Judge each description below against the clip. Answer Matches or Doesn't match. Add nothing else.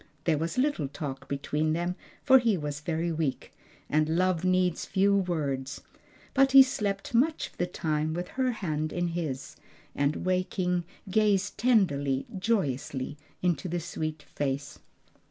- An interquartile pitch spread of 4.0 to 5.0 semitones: Matches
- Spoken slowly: Doesn't match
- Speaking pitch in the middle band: Matches